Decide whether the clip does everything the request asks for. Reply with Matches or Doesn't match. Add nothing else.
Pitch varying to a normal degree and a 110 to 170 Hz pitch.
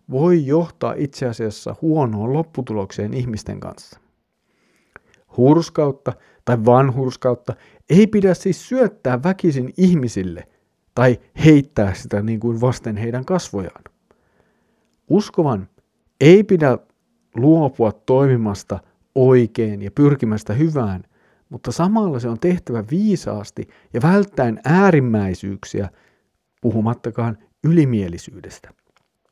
Doesn't match